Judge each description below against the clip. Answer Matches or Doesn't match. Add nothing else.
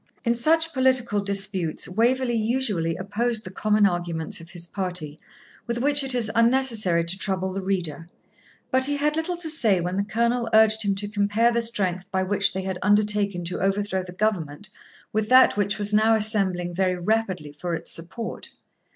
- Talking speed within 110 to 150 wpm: Doesn't match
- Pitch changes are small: Doesn't match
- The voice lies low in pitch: Doesn't match